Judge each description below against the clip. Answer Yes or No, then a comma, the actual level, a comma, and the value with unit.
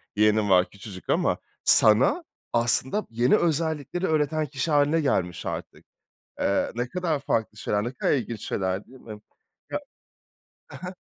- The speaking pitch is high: No, low, 125 Hz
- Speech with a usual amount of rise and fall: No, wide, 6.5 semitones